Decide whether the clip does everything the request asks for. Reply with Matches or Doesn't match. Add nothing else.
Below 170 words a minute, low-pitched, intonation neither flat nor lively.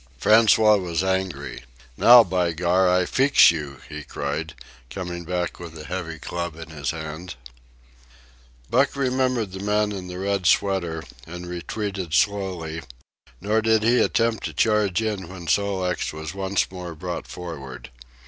Matches